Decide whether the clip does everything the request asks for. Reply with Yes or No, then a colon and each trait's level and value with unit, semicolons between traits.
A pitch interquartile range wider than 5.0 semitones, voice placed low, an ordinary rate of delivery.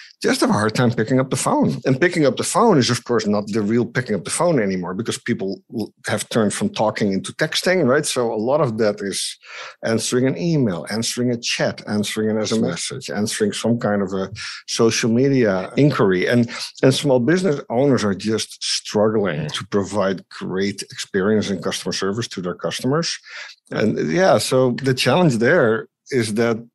No: average, 3.6 semitones; low, 115 Hz; average, 190 wpm